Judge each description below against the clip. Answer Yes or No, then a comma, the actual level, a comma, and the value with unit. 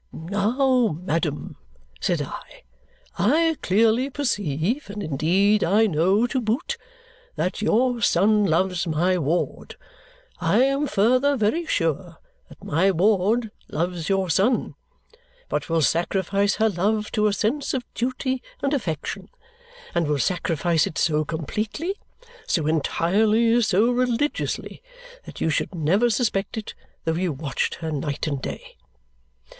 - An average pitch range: No, wide, 6.1 semitones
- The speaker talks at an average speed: No, slow, 130 wpm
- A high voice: Yes, high, 200 Hz